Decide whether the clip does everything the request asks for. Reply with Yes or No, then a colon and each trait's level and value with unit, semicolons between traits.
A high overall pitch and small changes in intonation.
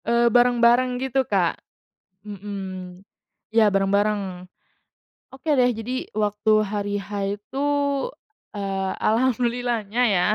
No: high, 215 Hz; average, 3.6 semitones